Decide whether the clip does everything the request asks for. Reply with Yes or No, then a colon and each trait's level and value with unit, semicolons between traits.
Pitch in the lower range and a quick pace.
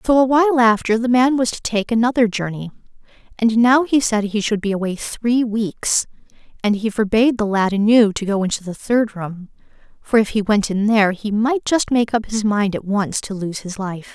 No: high, 220 Hz; fast, 220 wpm